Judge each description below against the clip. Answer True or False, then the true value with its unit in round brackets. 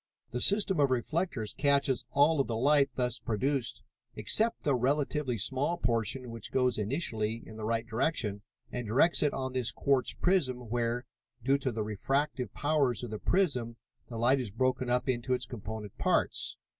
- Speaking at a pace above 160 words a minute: True (170 wpm)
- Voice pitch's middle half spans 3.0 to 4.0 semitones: True (3.4 semitones)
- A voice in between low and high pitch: False (125 Hz)